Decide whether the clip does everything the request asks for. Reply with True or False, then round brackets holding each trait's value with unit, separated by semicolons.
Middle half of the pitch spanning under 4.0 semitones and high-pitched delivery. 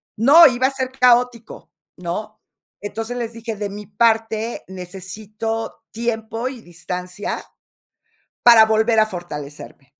True (2.8 semitones; 220 Hz)